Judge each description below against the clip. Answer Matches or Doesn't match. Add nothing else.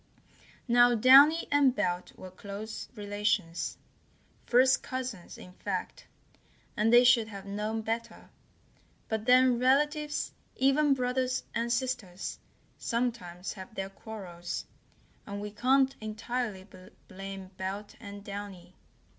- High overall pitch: Matches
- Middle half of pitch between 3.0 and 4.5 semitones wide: Matches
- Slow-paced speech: Matches